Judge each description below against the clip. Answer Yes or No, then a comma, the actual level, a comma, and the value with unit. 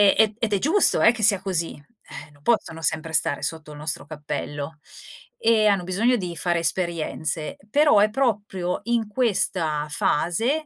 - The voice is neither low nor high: Yes, medium, 180 Hz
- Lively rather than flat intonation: Yes, wide, 5.9 semitones